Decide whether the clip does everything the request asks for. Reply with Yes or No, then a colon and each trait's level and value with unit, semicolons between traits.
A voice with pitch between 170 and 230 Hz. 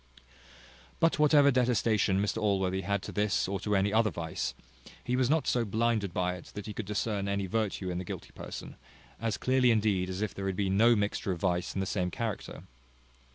No: low, 100 Hz